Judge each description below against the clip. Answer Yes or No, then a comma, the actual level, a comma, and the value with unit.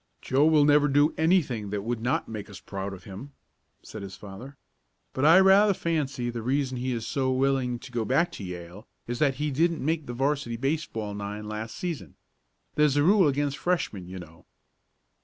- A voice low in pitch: Yes, low, 130 Hz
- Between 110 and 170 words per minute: No, average, 195 wpm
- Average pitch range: No, wide, 5.8 semitones